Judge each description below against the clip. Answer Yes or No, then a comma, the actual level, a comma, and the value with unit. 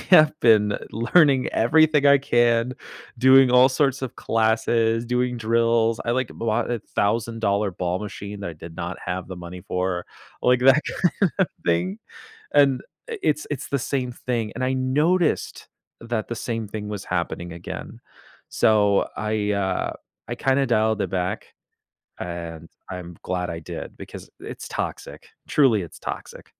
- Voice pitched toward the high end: No, low, 115 Hz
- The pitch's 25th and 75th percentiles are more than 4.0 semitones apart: Yes, average, 5.0 semitones